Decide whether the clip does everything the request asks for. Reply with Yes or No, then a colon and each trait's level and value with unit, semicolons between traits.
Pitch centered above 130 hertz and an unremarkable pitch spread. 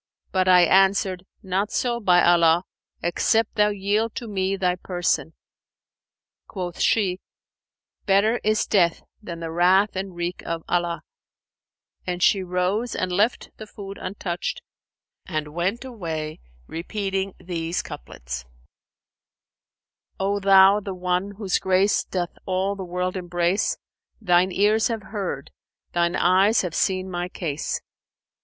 No: medium, 185 Hz; narrow, 2.3 semitones